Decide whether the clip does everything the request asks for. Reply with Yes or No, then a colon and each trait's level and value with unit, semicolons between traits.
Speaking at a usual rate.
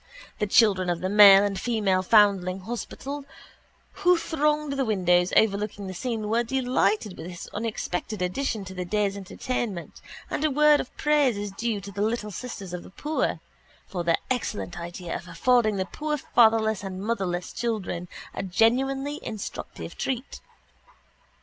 Yes: average, 155 wpm